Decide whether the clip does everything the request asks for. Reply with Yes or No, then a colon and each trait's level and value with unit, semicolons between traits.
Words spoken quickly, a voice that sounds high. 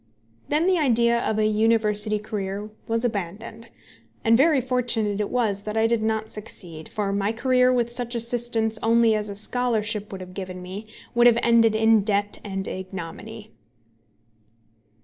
No: average, 160 wpm; high, 220 Hz